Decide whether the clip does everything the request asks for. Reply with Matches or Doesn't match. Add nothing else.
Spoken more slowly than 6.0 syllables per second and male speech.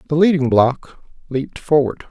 Matches